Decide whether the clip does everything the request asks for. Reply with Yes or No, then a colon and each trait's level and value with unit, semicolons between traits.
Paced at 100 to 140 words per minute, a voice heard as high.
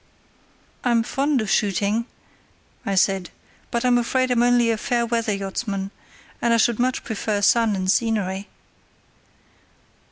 Yes: slow, 135 wpm; high, 230 Hz